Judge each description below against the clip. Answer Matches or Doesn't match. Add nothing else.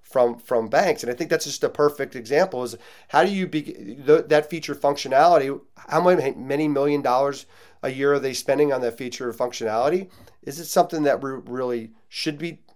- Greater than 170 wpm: Matches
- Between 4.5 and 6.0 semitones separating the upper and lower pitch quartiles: Doesn't match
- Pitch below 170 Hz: Matches